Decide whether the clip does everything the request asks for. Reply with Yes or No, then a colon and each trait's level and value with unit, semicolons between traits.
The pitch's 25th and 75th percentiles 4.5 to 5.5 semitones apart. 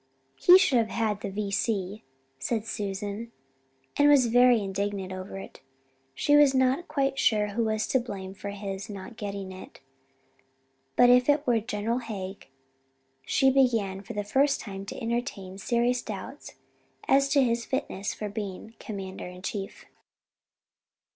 No: average, 4.0 semitones